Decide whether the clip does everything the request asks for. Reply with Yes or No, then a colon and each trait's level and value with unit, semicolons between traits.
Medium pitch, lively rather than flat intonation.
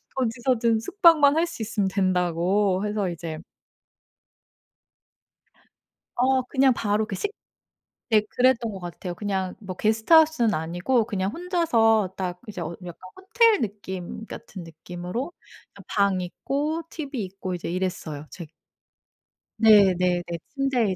No: high, 210 Hz; wide, 5.9 semitones